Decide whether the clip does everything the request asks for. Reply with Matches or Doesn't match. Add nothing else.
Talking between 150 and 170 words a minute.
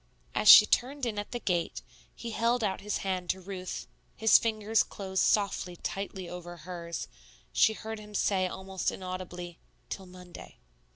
Matches